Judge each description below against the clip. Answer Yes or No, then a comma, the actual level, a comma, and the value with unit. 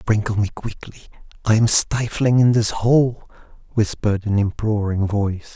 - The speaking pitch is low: Yes, low, 110 Hz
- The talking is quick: No, average, 140 wpm